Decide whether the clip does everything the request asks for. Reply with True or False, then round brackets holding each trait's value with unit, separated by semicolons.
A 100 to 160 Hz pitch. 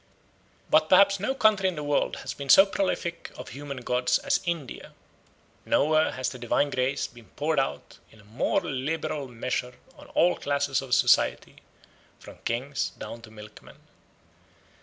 True (140 Hz)